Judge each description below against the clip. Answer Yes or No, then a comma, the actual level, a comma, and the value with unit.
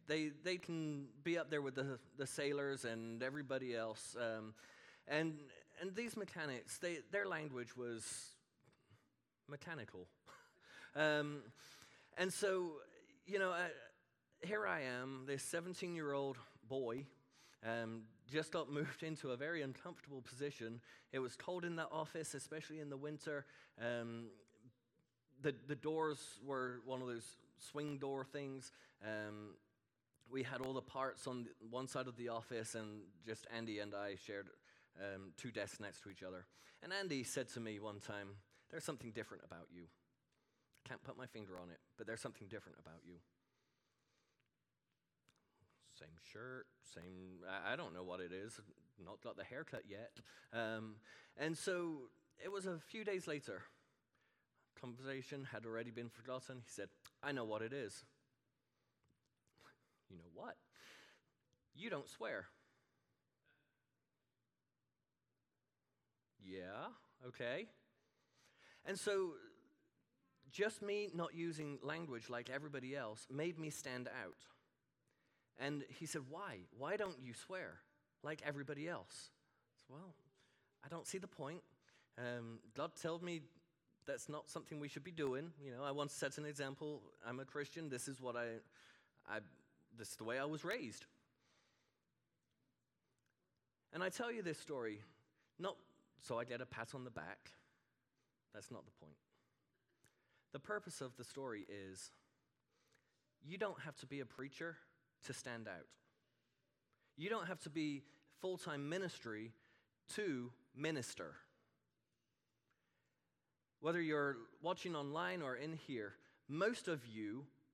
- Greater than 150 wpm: No, average, 145 wpm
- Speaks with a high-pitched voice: No, low, 135 Hz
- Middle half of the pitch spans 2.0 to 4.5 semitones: No, average, 5.2 semitones